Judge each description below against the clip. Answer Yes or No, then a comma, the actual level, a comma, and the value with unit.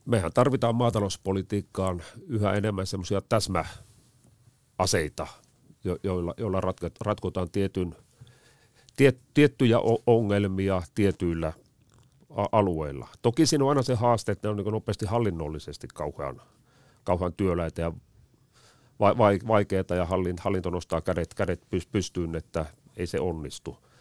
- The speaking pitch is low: Yes, low, 100 Hz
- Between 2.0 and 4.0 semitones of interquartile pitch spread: No, average, 4.6 semitones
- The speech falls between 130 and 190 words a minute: No, average, 100 wpm